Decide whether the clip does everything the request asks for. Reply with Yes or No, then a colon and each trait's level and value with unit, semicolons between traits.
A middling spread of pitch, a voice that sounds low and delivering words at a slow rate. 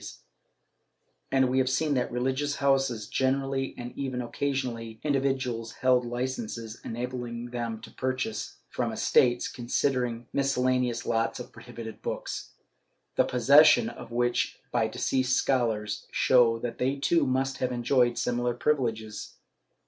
No: narrow, 2.1 semitones; low, 125 Hz; slow, 105 wpm